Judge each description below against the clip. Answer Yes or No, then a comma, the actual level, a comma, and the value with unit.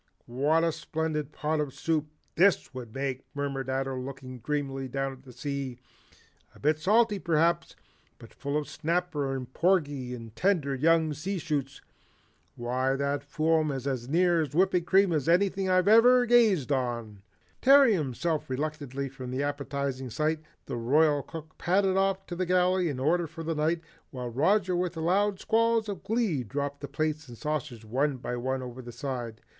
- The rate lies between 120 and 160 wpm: No, average, 170 wpm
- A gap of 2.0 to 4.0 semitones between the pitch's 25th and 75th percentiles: No, average, 4.7 semitones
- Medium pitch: Yes, medium, 150 Hz